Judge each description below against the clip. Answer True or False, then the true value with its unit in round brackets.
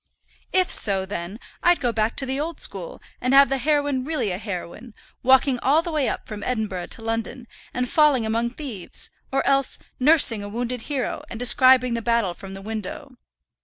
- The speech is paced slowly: False (190 wpm)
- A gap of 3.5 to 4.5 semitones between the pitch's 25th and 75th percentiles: True (4.0 semitones)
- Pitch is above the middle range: True (245 Hz)